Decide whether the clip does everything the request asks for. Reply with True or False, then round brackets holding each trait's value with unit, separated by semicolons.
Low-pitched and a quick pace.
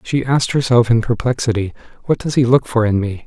True (120 Hz; 220 wpm)